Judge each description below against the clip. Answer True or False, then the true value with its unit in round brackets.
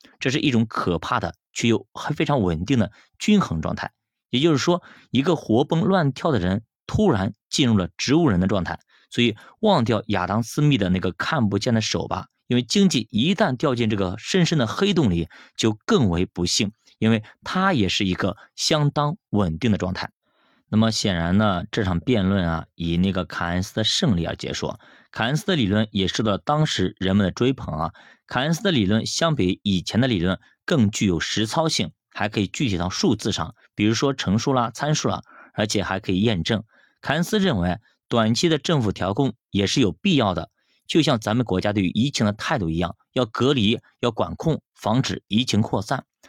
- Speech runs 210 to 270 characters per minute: False (290 characters per minute)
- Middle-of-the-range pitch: False (110 Hz)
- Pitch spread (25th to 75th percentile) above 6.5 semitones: True (7.0 semitones)